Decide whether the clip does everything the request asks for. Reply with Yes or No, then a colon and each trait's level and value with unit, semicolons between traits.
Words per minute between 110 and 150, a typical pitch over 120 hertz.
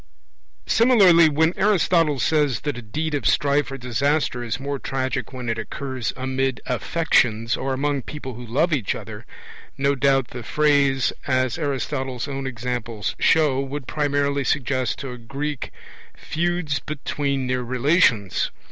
Yes: average, 145 wpm; low, 135 Hz